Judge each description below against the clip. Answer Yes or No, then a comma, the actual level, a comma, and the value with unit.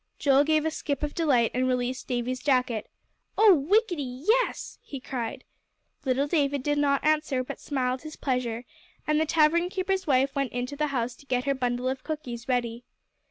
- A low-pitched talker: No, very high, 275 Hz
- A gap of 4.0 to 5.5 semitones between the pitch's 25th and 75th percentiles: No, average, 3.3 semitones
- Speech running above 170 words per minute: Yes, average, 180 wpm